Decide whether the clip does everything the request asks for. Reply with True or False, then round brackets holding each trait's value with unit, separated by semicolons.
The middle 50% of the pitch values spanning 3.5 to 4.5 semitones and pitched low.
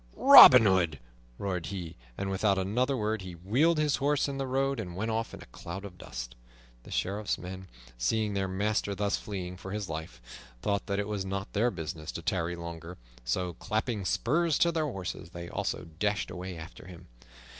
True (3.9 semitones; 95 Hz)